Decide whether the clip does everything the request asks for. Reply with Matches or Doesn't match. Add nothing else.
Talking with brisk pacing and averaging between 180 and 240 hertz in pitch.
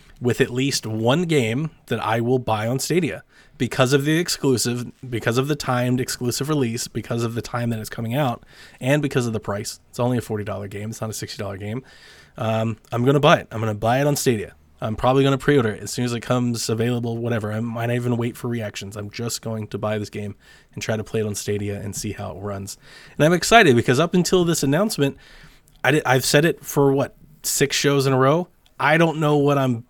Doesn't match